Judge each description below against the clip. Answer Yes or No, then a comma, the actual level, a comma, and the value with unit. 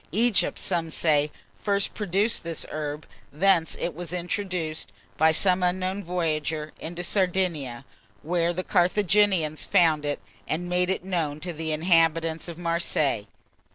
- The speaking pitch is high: No, medium, 170 Hz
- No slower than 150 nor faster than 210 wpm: No, slow, 135 wpm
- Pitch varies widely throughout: No, average, 2.8 semitones